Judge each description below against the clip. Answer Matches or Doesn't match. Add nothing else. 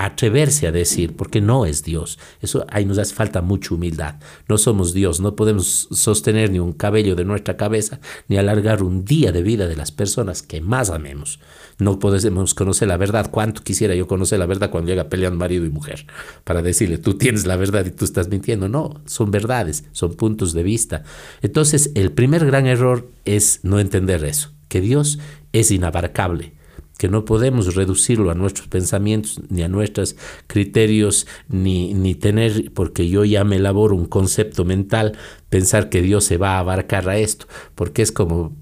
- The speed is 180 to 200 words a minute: Matches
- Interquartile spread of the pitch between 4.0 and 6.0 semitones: Doesn't match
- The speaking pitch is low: Matches